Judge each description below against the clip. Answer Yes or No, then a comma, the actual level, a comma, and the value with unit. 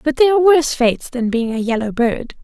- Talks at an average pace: No, fast, 245 wpm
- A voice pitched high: Yes, very high, 260 Hz